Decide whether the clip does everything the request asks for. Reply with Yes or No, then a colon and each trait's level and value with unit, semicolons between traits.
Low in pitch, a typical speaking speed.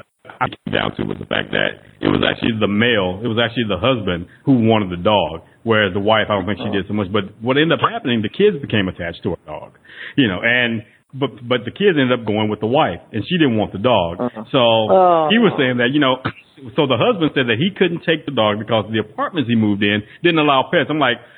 No: low, 120 Hz; fast, 260 wpm